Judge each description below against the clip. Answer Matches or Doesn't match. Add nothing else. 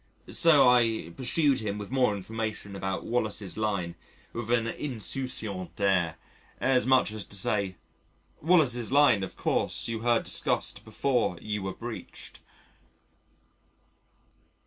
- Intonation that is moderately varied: Matches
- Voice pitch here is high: Doesn't match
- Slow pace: Matches